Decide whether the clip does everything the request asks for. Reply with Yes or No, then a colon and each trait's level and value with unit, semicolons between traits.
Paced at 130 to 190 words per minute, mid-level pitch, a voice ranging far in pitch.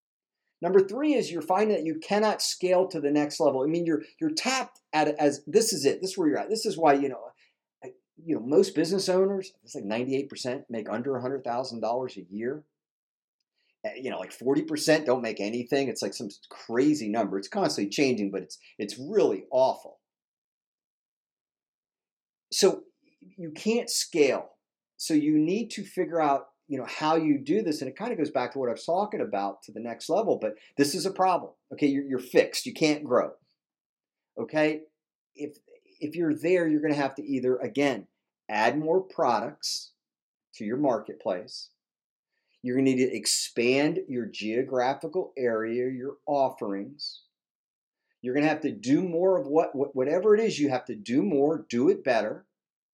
Yes: average, 185 wpm; medium, 155 Hz; wide, 6.5 semitones